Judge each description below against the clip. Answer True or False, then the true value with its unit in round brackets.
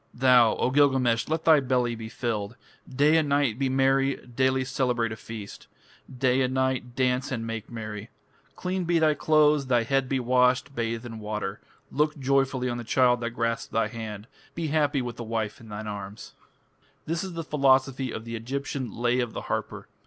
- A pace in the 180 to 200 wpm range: True (190 wpm)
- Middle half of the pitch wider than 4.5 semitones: False (3.0 semitones)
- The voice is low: True (125 Hz)